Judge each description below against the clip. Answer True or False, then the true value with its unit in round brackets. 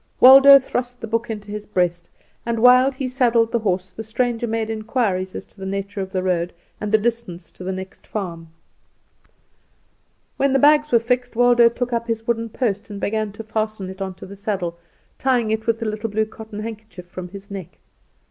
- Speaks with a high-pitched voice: True (220 Hz)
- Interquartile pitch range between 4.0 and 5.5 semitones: False (3.5 semitones)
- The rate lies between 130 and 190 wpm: False (205 wpm)